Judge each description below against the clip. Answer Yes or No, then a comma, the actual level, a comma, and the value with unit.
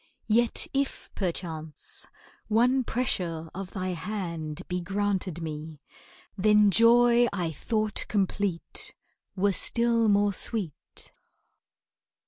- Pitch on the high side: Yes, high, 200 Hz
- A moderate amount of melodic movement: Yes, average, 4.7 semitones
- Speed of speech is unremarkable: No, slow, 100 wpm